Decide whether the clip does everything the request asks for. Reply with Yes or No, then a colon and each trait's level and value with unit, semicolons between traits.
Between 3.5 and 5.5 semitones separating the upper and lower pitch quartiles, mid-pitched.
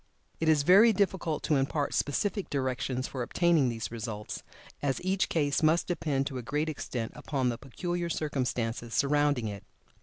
Yes: average, 4.5 semitones; medium, 145 Hz